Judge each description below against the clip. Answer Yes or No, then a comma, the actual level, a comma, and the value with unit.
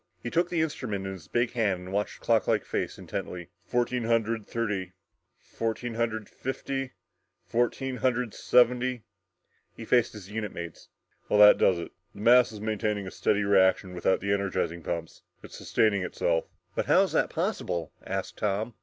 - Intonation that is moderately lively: Yes, average, 4.0 semitones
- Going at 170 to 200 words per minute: Yes, average, 175 wpm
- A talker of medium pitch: No, low, 105 Hz